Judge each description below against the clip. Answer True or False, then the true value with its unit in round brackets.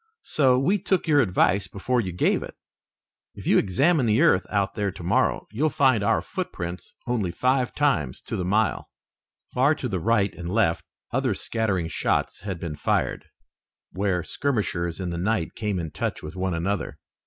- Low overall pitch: True (100 Hz)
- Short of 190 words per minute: True (175 wpm)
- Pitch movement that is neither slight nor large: False (6.1 semitones)